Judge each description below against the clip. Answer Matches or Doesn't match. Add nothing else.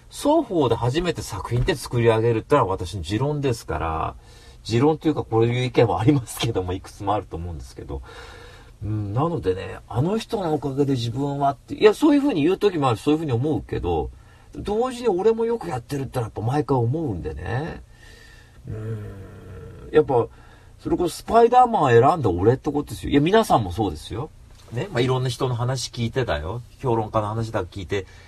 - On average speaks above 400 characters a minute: Matches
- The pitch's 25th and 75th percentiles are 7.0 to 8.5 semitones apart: Doesn't match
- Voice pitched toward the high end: Doesn't match